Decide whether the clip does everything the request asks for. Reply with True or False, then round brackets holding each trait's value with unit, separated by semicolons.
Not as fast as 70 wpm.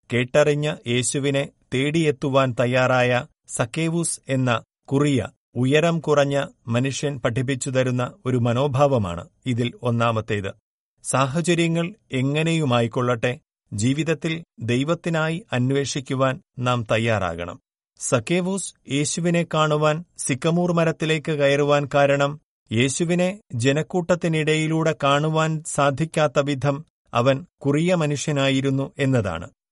False (80 wpm)